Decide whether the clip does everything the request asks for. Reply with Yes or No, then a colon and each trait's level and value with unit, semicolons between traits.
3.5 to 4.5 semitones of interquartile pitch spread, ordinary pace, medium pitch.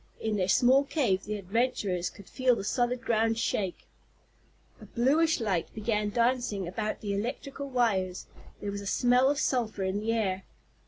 No: average, 3.9 semitones; average, 165 wpm; high, 220 Hz